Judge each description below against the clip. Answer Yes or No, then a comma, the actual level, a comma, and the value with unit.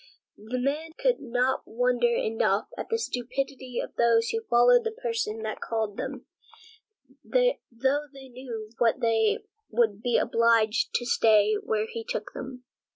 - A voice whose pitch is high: Yes, high, 245 Hz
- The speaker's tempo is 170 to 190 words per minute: No, average, 150 wpm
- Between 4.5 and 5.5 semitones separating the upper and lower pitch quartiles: No, average, 3.4 semitones